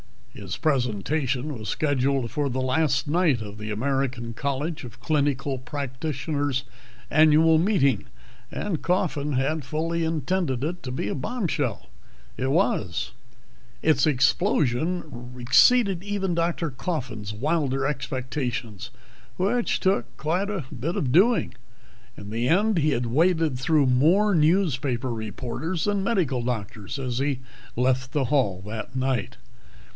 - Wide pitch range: No, average, 4.7 semitones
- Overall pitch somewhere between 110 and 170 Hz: Yes, medium, 140 Hz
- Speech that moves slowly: Yes, slow, 130 wpm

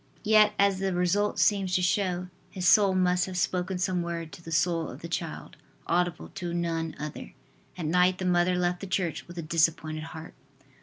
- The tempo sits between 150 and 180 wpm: No, average, 195 wpm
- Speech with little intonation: Yes, narrow, 1.9 semitones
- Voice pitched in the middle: Yes, medium, 180 Hz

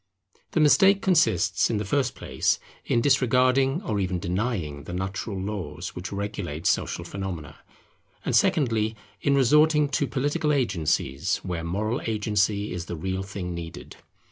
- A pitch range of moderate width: No, wide, 6.6 semitones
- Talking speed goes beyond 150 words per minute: No, average, 145 wpm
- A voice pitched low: Yes, low, 105 Hz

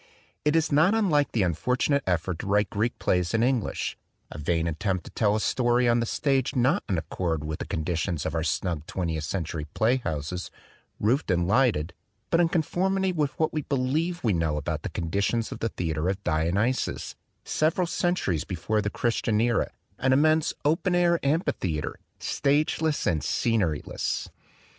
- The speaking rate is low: No, average, 175 wpm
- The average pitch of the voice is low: Yes, low, 110 Hz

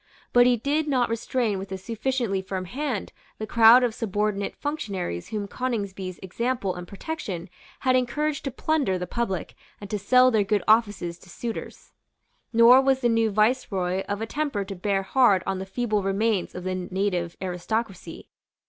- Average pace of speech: Yes, average, 170 wpm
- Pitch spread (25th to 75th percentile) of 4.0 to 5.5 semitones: Yes, average, 4.4 semitones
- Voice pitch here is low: No, high, 215 Hz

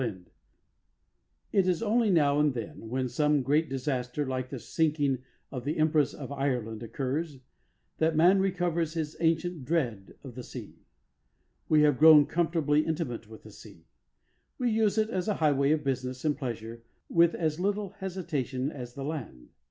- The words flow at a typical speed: Yes, average, 170 wpm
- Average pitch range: Yes, average, 4.5 semitones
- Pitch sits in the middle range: Yes, medium, 150 Hz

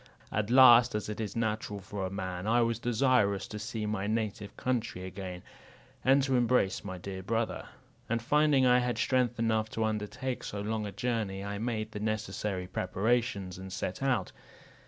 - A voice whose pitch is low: Yes, low, 110 Hz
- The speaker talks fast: No, average, 175 wpm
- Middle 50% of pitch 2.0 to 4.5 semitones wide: Yes, average, 3.3 semitones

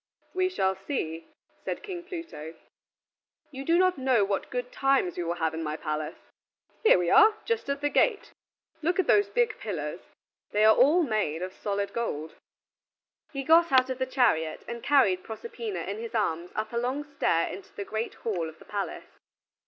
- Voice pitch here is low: No, high, 230 Hz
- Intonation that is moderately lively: No, wide, 8.5 semitones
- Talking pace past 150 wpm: Yes, average, 185 wpm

